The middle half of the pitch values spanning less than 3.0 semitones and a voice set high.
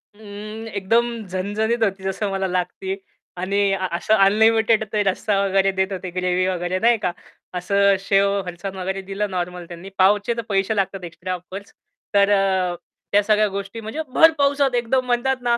Yes: narrow, 2.6 semitones; high, 195 Hz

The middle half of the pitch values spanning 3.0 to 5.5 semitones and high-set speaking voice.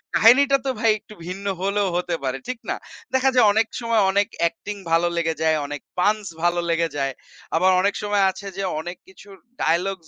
Yes: average, 4.1 semitones; high, 195 Hz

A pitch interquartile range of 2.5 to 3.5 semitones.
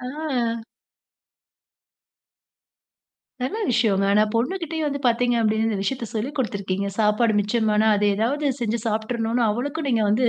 Yes: average, 3.1 semitones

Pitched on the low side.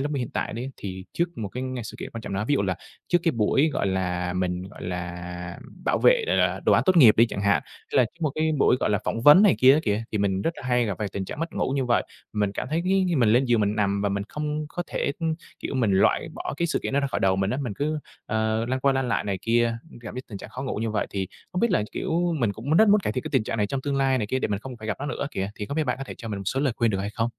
Yes: low, 115 Hz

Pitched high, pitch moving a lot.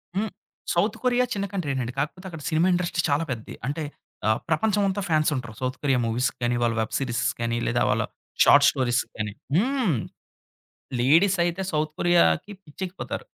No: medium, 155 Hz; wide, 6.8 semitones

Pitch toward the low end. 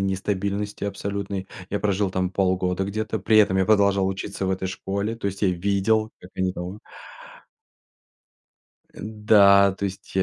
Yes: low, 100 Hz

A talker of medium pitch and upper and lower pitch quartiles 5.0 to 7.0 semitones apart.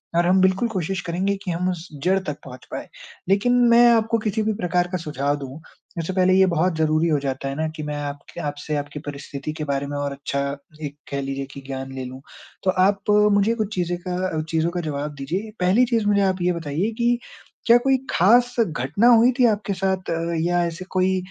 Yes: medium, 175 Hz; average, 5.3 semitones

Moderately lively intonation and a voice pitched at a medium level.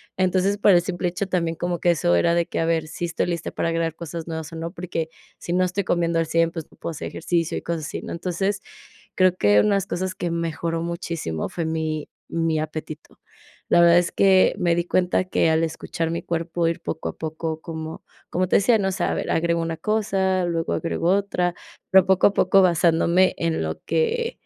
No: narrow, 2.0 semitones; medium, 170 Hz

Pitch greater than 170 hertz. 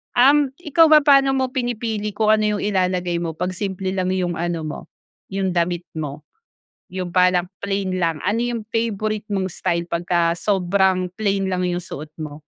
Yes: high, 190 Hz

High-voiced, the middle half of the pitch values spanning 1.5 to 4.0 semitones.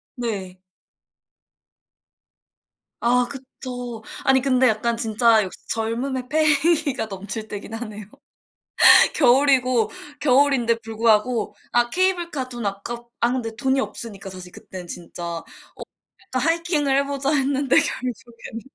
Yes: high, 245 Hz; average, 3.5 semitones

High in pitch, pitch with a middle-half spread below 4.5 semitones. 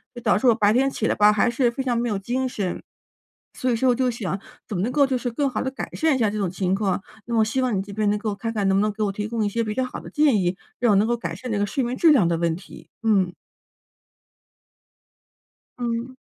Yes: high, 220 Hz; average, 3.6 semitones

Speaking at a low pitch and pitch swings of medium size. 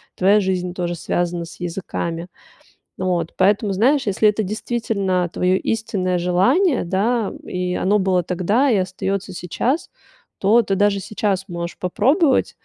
No: high, 190 Hz; average, 3.1 semitones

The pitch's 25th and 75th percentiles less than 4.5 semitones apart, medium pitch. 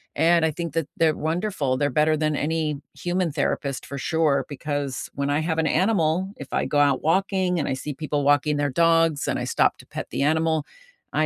Yes: narrow, 2.4 semitones; medium, 155 Hz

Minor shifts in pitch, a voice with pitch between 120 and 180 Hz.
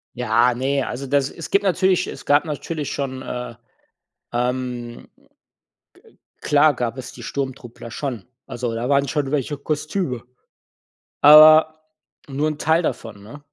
No: average, 3.7 semitones; medium, 140 Hz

